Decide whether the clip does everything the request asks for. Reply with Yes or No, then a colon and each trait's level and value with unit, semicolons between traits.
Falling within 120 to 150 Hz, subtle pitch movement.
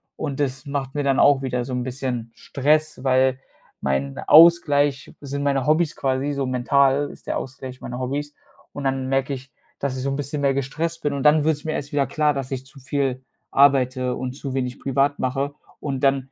Yes: low, 135 Hz; narrow, 1.7 semitones